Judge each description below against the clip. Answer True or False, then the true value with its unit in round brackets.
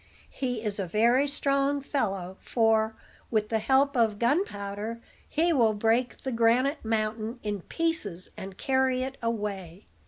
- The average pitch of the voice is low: False (230 Hz)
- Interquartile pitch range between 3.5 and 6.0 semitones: True (4.0 semitones)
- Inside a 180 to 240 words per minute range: False (145 wpm)